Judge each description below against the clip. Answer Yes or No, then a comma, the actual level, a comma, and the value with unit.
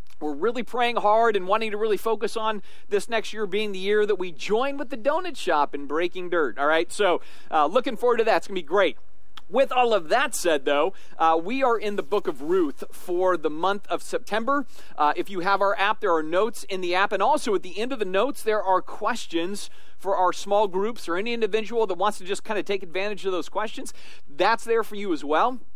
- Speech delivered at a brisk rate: Yes, fast, 245 wpm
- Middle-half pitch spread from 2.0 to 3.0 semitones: No, average, 3.4 semitones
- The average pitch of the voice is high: Yes, high, 210 Hz